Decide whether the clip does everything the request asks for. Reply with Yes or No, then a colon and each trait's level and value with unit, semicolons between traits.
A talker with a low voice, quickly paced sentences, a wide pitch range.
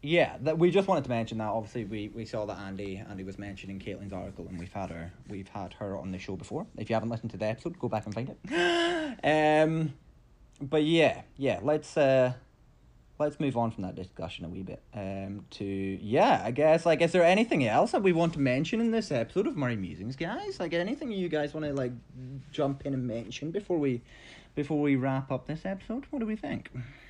Yes: low, 125 Hz; fast, 225 wpm; wide, 7.5 semitones